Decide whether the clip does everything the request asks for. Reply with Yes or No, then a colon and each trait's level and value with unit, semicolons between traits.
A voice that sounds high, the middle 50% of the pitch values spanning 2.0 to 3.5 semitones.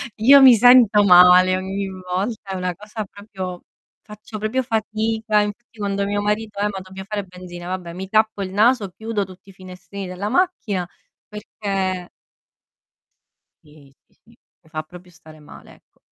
Yes: high, 200 Hz; average, 2.8 semitones